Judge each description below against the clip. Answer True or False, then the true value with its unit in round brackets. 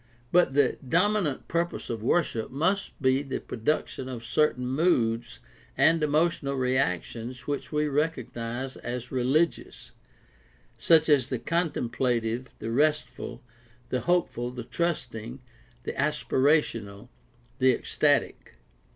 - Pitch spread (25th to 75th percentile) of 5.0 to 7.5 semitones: False (4.2 semitones)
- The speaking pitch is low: True (130 Hz)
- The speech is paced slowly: True (115 wpm)